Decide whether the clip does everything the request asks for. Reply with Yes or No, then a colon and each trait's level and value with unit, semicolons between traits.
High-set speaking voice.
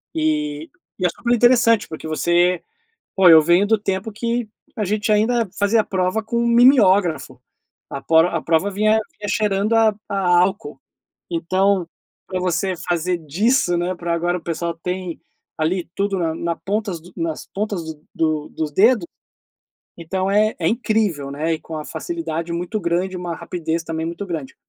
No: medium, 180 Hz